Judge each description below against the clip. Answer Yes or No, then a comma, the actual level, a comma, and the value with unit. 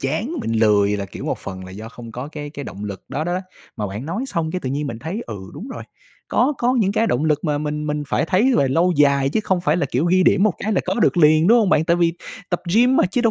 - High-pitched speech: No, medium, 155 Hz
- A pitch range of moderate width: No, wide, 6.3 semitones